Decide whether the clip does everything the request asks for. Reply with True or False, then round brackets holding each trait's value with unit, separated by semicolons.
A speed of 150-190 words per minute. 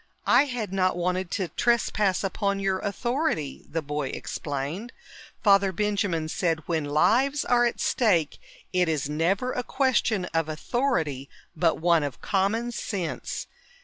False (140 wpm)